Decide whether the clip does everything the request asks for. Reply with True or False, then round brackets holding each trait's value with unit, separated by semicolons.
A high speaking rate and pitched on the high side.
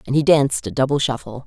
False (245 wpm; 130 Hz)